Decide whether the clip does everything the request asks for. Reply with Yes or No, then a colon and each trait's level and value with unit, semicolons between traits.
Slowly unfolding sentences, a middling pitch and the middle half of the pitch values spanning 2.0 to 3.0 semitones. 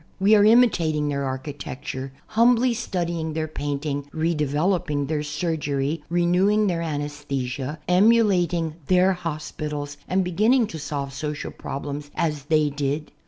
No: slow, 120 wpm; medium, 155 Hz; average, 3.9 semitones